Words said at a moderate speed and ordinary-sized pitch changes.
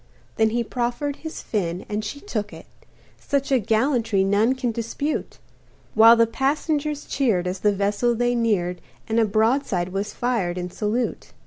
Yes: average, 160 wpm; average, 3.8 semitones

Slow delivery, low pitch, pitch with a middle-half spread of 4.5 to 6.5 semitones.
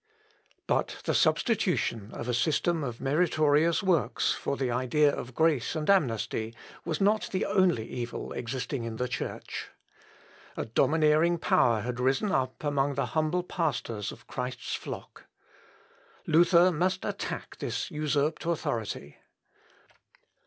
No: slow, 130 wpm; medium, 145 Hz; average, 5.3 semitones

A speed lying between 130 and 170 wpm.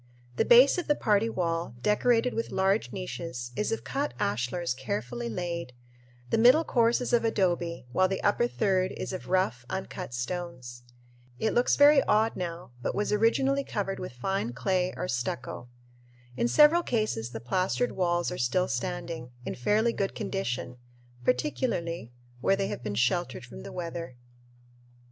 Yes: average, 160 wpm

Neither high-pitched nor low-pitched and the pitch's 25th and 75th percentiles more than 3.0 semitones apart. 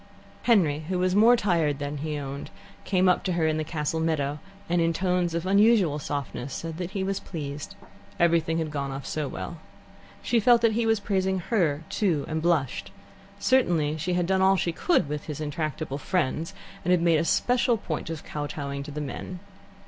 Yes: medium, 165 Hz; average, 4.1 semitones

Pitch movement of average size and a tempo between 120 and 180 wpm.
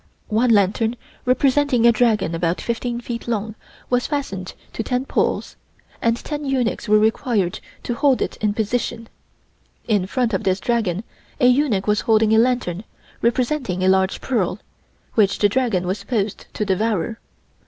Yes: average, 3.7 semitones; average, 155 wpm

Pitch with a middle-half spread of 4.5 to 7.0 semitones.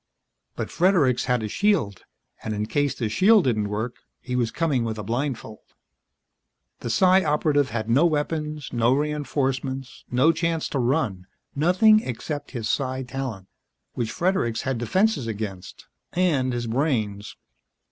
Yes: average, 5.0 semitones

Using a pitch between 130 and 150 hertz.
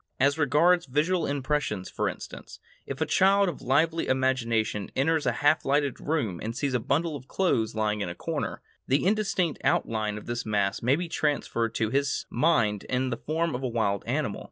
Yes: low, 135 Hz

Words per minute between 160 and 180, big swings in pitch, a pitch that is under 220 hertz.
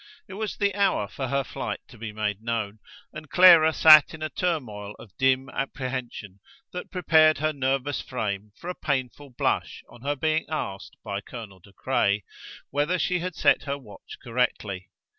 Yes: average, 175 wpm; wide, 6.6 semitones; low, 135 Hz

